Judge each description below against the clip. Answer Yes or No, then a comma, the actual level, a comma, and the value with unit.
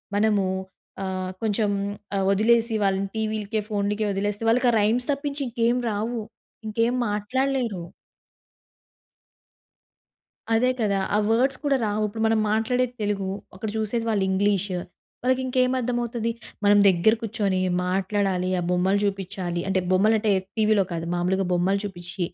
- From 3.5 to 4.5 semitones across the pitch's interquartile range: No, average, 3.0 semitones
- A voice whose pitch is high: Yes, high, 210 Hz